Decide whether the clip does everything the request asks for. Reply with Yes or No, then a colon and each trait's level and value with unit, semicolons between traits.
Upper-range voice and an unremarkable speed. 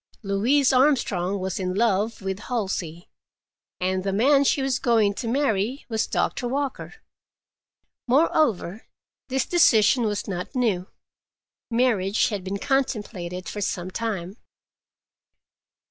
No: high, 215 Hz; slow, 115 wpm